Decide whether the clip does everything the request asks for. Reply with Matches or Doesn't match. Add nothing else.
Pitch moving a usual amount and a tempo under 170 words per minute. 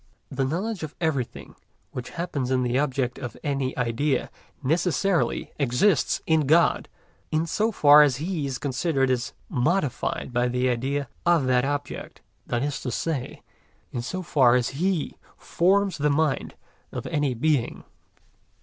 Matches